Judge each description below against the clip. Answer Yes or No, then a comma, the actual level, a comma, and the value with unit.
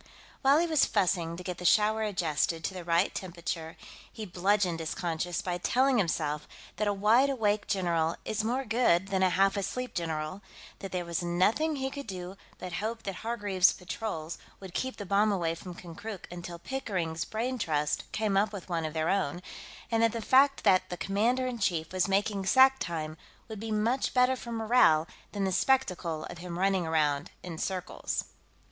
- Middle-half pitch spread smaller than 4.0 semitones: No, average, 4.5 semitones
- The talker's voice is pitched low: No, high, 190 Hz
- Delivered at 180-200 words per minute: Yes, average, 190 wpm